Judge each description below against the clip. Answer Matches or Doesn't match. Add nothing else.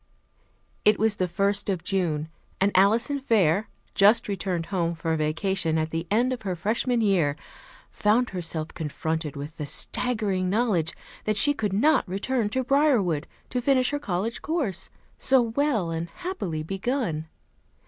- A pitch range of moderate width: Doesn't match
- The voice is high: Matches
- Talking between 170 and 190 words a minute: Doesn't match